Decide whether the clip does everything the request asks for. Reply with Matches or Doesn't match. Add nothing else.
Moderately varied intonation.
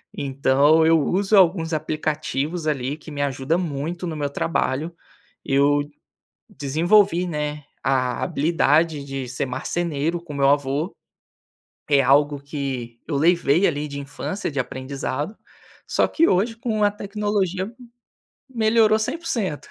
Matches